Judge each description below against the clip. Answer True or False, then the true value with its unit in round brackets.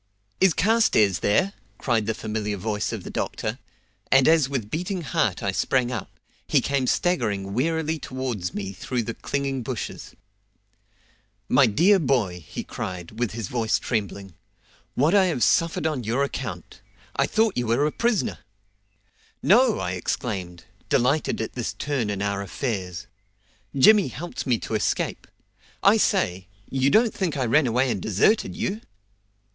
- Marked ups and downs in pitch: True (7.1 semitones)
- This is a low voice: True (125 Hz)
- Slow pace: False (155 wpm)